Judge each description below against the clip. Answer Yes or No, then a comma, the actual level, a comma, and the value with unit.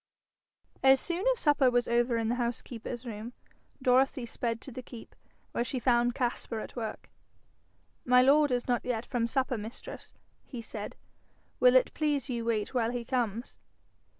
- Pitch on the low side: No, high, 245 Hz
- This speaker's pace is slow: No, average, 165 wpm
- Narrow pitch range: Yes, narrow, 1.8 semitones